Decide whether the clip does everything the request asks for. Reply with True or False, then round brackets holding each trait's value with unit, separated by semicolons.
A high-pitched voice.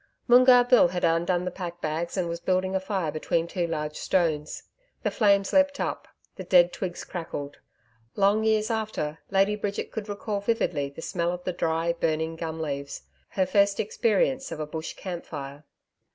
False (180 Hz)